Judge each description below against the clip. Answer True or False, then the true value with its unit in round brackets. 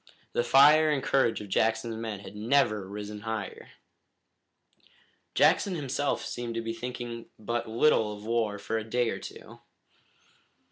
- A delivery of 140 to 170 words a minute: True (145 wpm)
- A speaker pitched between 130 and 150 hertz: False (115 Hz)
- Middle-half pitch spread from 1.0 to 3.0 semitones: True (2.6 semitones)